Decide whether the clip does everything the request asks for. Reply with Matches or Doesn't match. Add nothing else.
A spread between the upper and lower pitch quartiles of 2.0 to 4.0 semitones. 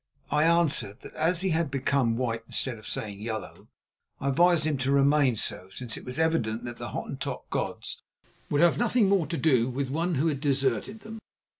Doesn't match